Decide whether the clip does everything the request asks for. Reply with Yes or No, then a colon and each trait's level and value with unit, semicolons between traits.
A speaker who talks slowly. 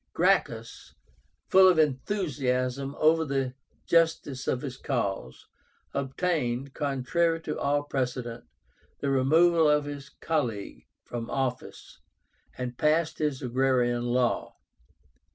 Yes: slow, 105 wpm